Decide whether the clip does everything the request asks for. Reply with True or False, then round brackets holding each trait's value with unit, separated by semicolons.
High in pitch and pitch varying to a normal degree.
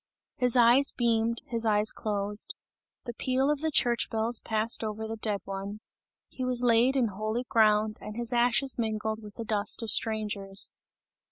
False (225 Hz; 2.2 semitones)